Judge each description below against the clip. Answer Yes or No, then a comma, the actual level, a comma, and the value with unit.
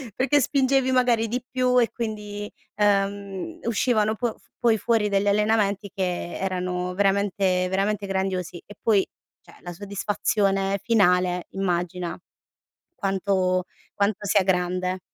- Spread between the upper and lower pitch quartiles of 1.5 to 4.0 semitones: Yes, average, 2.9 semitones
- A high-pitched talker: Yes, high, 200 Hz